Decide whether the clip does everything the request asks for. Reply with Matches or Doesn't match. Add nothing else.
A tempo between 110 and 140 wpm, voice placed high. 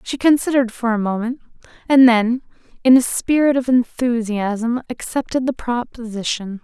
Matches